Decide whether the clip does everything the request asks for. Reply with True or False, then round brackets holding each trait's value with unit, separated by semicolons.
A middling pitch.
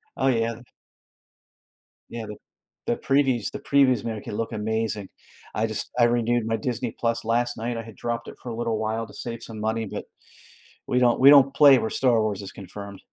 False (115 Hz)